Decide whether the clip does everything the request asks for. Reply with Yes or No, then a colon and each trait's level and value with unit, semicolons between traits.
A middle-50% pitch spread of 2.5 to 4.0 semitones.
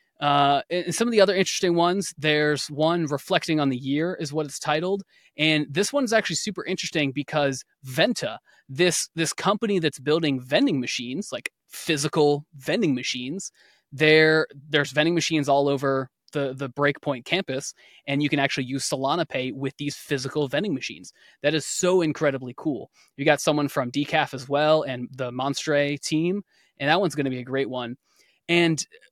Yes: average, 2.8 semitones